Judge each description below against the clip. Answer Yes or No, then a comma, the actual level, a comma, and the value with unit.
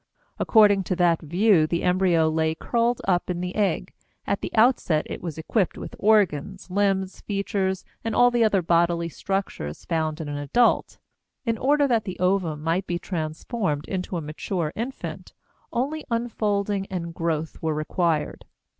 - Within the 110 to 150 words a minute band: No, average, 160 wpm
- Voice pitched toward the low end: No, medium, 185 Hz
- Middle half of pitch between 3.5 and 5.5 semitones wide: Yes, average, 4.2 semitones